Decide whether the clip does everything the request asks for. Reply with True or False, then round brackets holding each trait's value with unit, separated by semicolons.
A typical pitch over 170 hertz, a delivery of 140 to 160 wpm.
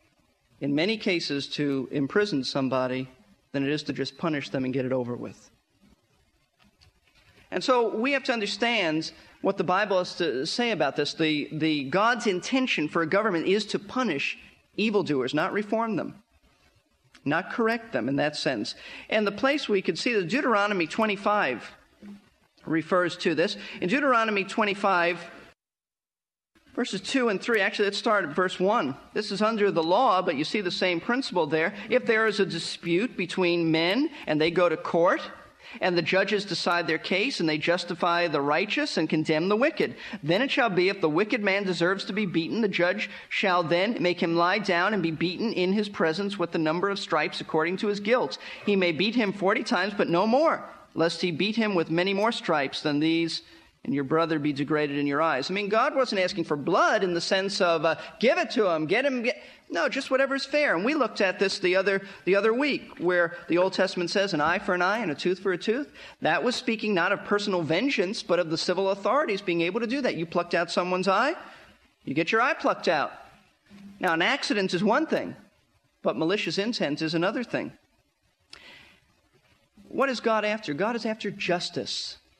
False (190 Hz; 200 wpm)